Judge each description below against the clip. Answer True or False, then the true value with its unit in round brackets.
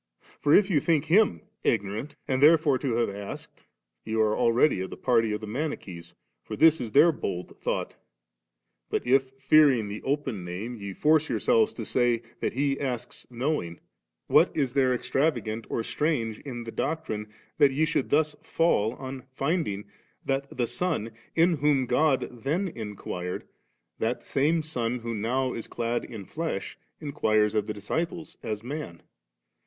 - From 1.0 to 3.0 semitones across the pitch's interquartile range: False (5.6 semitones)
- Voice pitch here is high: False (130 Hz)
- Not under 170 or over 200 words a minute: False (160 wpm)